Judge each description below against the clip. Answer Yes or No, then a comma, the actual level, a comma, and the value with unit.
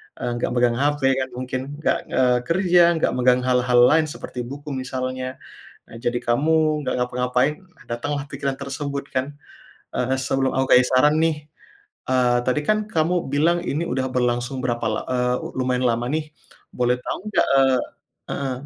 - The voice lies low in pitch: Yes, low, 130 Hz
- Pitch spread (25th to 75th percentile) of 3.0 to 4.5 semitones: No, narrow, 2.6 semitones